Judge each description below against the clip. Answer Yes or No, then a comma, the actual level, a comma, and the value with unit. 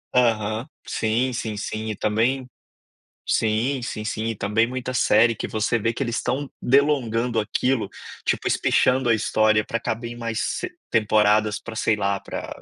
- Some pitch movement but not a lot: No, narrow, 2.3 semitones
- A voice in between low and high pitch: No, low, 115 Hz